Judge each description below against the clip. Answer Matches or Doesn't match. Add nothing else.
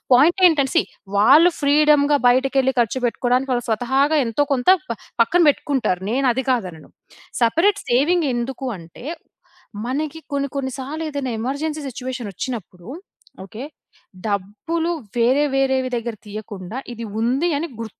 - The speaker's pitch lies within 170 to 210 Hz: Doesn't match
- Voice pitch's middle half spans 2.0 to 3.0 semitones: Doesn't match